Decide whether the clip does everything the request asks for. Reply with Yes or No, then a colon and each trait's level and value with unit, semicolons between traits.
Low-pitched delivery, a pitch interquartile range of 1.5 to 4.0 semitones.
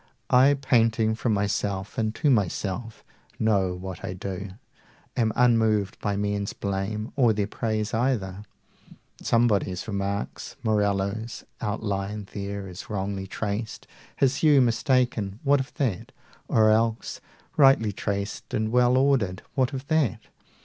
Yes: low, 110 Hz; average, 3.4 semitones